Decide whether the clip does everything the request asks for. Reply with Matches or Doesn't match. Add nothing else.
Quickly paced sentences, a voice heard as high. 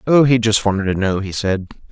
Doesn't match